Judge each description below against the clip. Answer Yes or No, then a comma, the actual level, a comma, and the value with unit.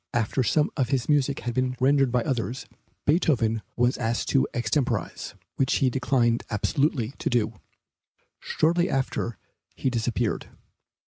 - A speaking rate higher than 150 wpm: No, slow, 135 wpm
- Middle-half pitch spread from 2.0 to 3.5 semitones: Yes, narrow, 2.6 semitones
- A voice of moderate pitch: No, low, 125 Hz